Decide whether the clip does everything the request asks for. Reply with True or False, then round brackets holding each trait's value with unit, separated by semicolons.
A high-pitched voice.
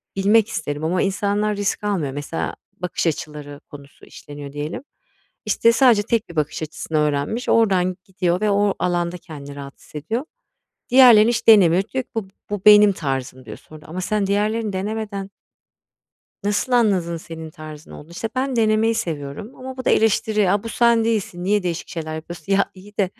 True (195 Hz)